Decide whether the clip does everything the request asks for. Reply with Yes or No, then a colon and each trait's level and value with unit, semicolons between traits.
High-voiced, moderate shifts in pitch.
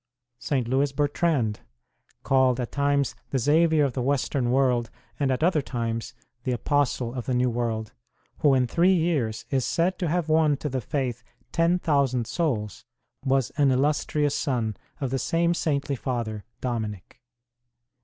No: low, 135 Hz; average, 3.5 semitones